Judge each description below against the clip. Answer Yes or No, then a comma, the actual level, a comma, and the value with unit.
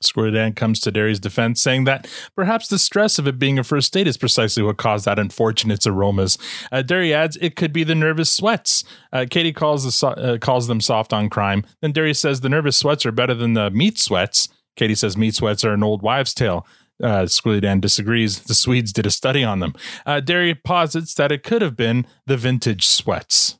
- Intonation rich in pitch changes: Yes, wide, 5.7 semitones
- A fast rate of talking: Yes, fast, 220 wpm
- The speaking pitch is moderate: No, low, 125 Hz